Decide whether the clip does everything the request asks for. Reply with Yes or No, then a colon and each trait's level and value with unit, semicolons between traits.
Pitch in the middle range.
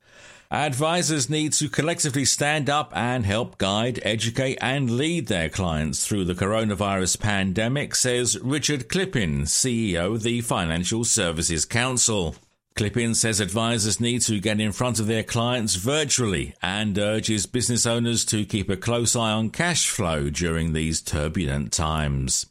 No: low, 110 Hz